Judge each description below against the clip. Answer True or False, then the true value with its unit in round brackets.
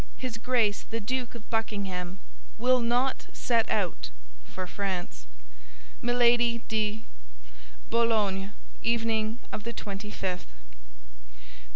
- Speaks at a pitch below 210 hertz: False (220 Hz)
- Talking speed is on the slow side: True (105 wpm)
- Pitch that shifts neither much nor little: True (3.4 semitones)